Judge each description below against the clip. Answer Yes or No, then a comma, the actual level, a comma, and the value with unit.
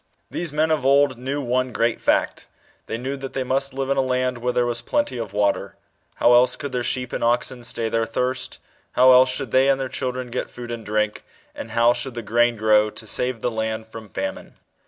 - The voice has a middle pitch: No, low, 125 Hz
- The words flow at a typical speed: No, fast, 225 wpm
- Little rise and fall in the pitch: Yes, narrow, 2.3 semitones